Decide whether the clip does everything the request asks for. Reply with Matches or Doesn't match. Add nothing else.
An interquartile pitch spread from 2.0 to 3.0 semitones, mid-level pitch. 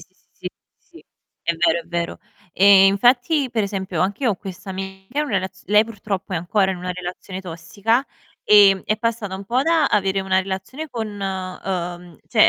Doesn't match